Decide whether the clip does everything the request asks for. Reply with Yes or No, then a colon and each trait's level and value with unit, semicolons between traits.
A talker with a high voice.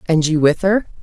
No: medium, 170 Hz